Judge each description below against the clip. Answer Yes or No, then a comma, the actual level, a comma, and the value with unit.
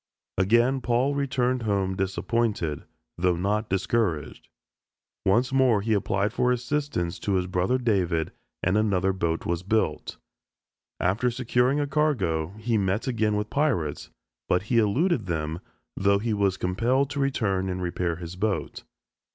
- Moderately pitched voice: No, low, 105 Hz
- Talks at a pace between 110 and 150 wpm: Yes, average, 145 wpm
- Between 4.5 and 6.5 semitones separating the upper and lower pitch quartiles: Yes, average, 5.0 semitones